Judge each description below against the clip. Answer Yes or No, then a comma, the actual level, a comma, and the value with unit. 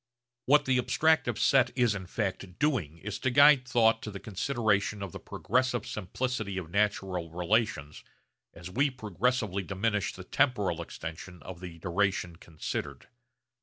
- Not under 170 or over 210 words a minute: No, average, 145 wpm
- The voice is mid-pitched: No, low, 105 Hz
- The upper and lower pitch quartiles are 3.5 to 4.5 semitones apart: No, wide, 5.5 semitones